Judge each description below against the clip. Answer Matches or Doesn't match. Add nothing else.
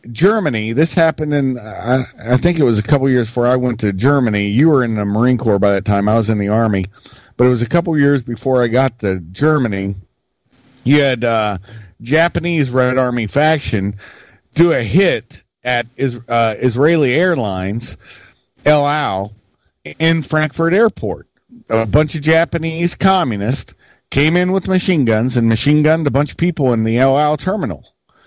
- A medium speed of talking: Matches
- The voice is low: Matches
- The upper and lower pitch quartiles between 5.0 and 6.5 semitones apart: Matches